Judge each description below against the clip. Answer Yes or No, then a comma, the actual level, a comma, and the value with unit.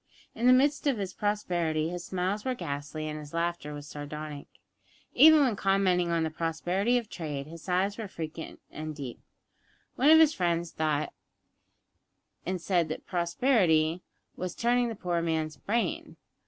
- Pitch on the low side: No, medium, 175 Hz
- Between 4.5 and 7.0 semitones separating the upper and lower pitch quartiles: Yes, average, 5.1 semitones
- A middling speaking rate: Yes, average, 160 wpm